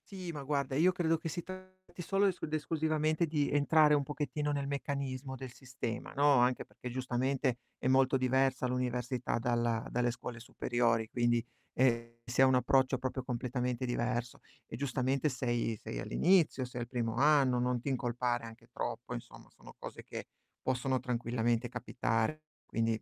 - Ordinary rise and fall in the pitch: Yes, average, 3.0 semitones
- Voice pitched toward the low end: Yes, low, 130 Hz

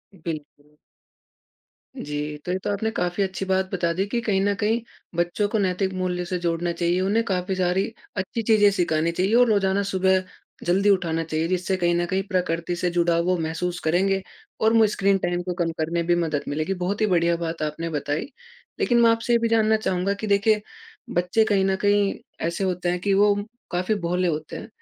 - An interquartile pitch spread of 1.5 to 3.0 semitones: Yes, average, 2.7 semitones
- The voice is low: No, medium, 185 Hz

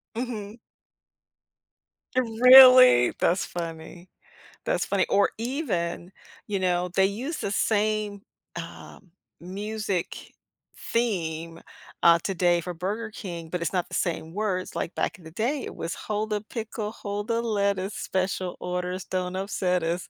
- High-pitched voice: Yes, high, 195 Hz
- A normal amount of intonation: Yes, average, 3.5 semitones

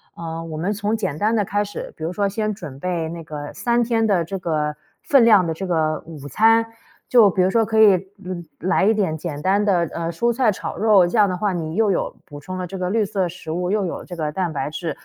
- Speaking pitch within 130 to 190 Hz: Yes, medium, 185 Hz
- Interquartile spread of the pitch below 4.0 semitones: No, average, 4.3 semitones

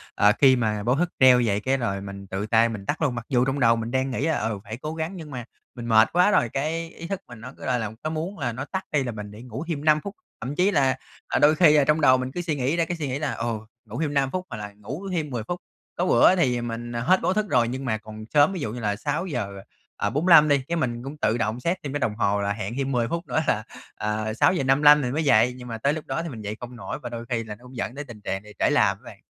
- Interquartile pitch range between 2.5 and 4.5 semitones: No, average, 5.2 semitones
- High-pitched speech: No, low, 130 Hz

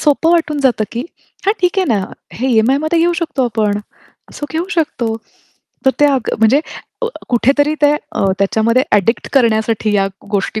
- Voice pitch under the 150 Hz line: No, very high, 255 Hz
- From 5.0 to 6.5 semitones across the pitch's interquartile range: Yes, wide, 5.4 semitones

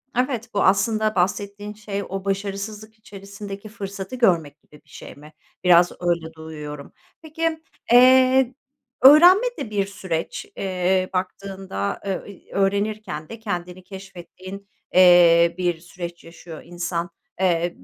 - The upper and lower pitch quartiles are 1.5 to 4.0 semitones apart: Yes, average, 3.5 semitones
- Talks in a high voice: Yes, high, 195 Hz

